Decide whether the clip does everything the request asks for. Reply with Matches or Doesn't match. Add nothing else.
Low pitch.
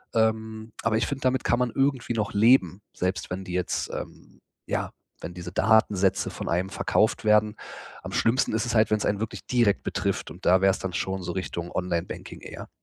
Matches